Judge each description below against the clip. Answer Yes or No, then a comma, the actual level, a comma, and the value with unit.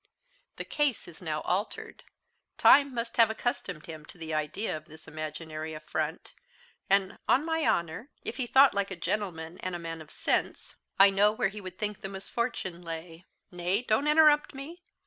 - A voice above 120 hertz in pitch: Yes, high, 190 Hz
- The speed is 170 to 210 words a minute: Yes, average, 180 wpm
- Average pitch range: No, wide, 6.4 semitones